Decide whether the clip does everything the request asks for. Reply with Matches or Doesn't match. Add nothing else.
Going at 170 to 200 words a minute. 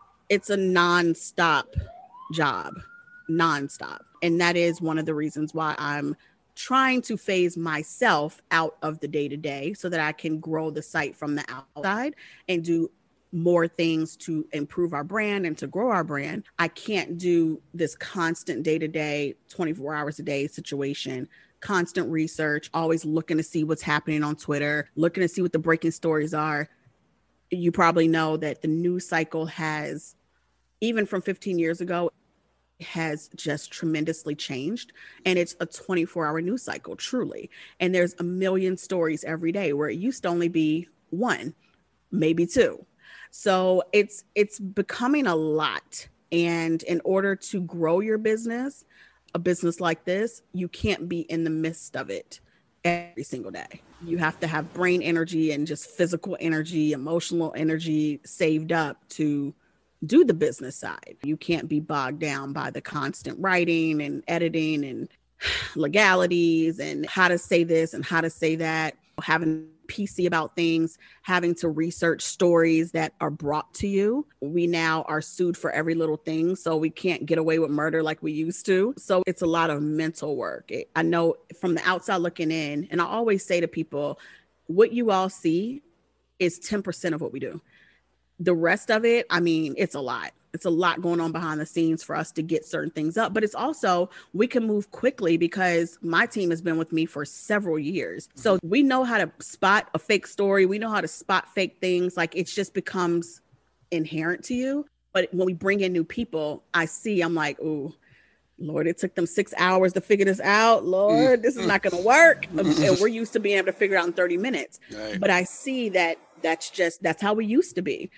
Matches